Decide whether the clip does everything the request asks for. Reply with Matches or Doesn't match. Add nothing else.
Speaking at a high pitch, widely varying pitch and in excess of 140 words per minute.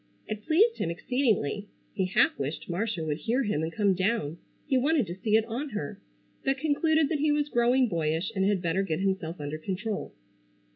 Matches